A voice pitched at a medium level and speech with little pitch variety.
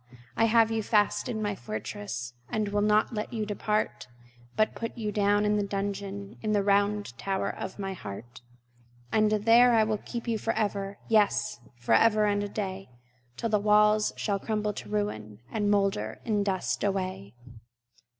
No: high, 205 Hz; narrow, 1.6 semitones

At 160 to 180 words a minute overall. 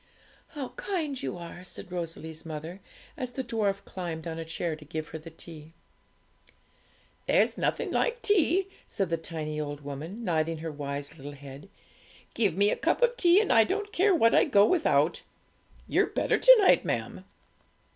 Yes: average, 175 wpm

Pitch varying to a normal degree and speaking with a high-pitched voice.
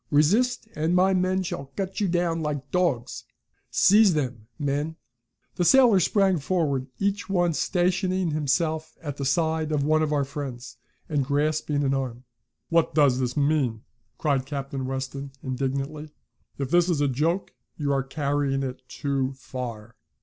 No: average, 4.2 semitones; medium, 150 Hz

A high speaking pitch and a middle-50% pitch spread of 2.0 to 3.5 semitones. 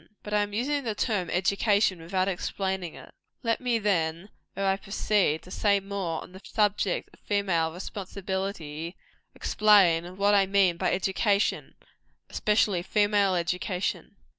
Yes: high, 195 Hz; narrow, 2.4 semitones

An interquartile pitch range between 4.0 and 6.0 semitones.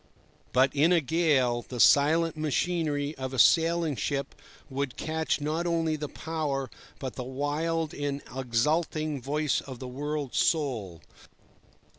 No: average, 3.2 semitones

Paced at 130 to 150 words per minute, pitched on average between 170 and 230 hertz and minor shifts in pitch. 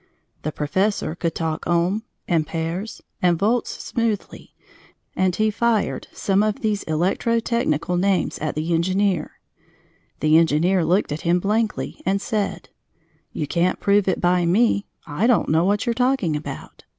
No: average, 145 wpm; medium, 185 Hz; average, 4.3 semitones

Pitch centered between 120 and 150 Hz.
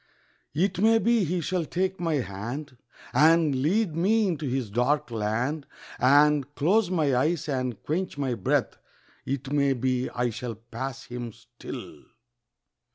Yes: medium, 140 Hz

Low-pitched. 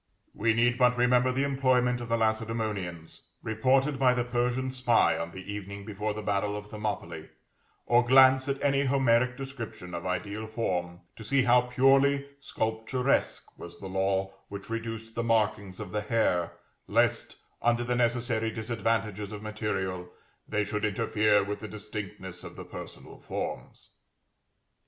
Yes: low, 110 Hz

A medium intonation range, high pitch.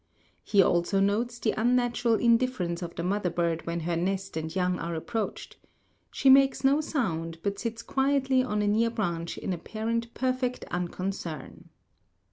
No: wide, 5.9 semitones; high, 205 Hz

